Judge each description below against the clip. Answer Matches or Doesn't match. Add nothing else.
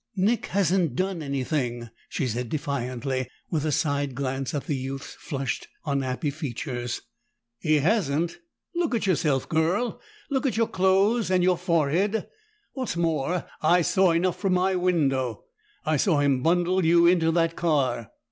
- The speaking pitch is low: Doesn't match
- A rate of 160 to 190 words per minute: Doesn't match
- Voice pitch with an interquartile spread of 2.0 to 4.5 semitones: Doesn't match